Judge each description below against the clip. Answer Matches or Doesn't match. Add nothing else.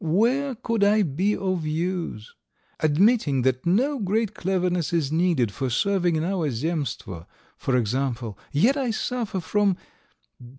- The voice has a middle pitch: Matches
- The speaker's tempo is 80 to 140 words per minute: Matches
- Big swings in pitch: Matches